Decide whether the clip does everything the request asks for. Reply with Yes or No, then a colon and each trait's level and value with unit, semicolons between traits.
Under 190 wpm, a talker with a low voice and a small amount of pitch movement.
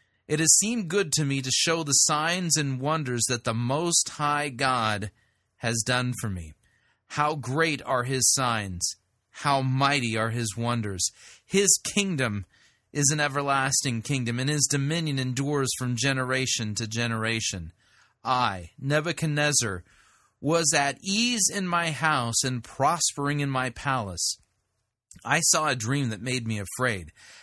No: average, 145 wpm; low, 130 Hz; average, 4.6 semitones